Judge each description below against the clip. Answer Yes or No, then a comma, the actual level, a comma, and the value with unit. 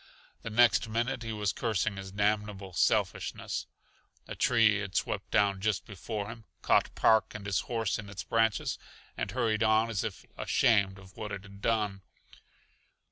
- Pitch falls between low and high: No, low, 105 Hz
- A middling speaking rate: Yes, average, 165 wpm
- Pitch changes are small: Yes, narrow, 2.2 semitones